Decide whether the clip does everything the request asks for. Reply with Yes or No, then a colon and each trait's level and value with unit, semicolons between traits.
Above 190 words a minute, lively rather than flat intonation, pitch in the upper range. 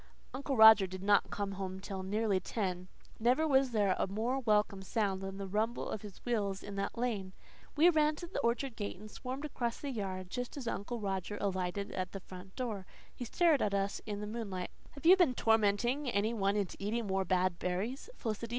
No: average, 200 wpm; average, 3.9 semitones; high, 210 Hz